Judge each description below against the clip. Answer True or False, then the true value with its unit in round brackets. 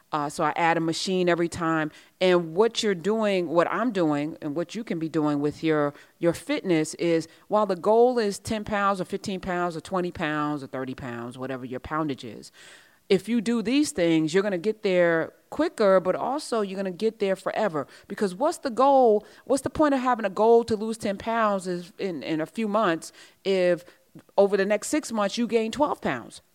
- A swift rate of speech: True (215 wpm)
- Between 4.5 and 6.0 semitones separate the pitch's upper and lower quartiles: True (5.4 semitones)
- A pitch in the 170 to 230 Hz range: True (190 Hz)